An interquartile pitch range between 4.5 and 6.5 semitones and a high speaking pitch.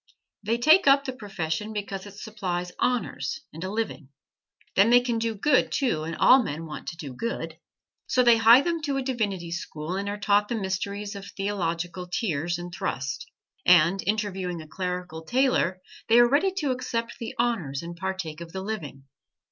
Yes: average, 5.3 semitones; high, 200 Hz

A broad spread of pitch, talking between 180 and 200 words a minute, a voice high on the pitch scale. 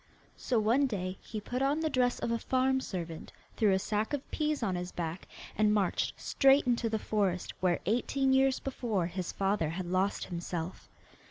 Yes: wide, 5.9 semitones; average, 185 wpm; high, 215 Hz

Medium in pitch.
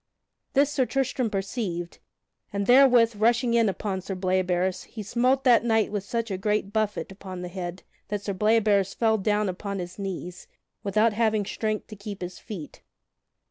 No: high, 205 Hz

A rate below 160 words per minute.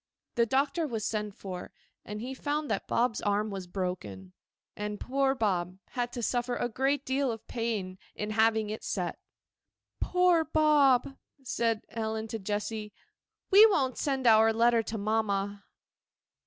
Yes: average, 150 wpm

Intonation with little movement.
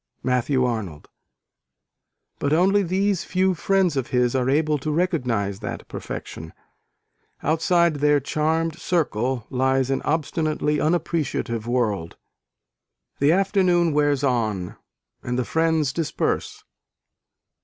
No: average, 4.8 semitones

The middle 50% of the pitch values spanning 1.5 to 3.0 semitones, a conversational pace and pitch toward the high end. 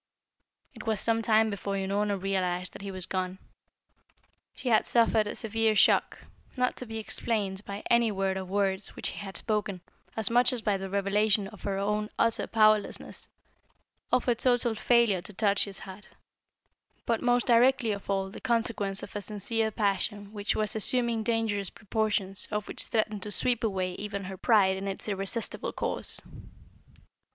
Yes: narrow, 2.4 semitones; average, 170 wpm; high, 210 Hz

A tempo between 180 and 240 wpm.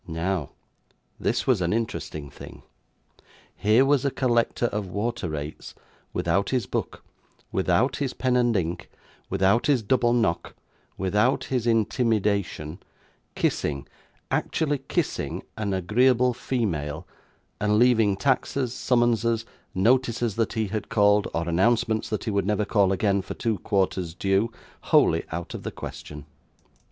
No: slow, 135 wpm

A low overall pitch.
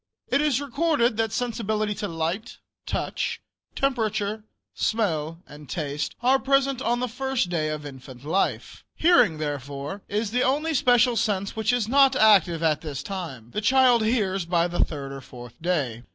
No: high, 205 Hz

